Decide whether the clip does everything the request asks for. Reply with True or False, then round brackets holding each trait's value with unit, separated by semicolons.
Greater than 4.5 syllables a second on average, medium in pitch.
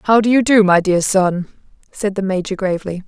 False (5.4 syllables/s; 195 Hz)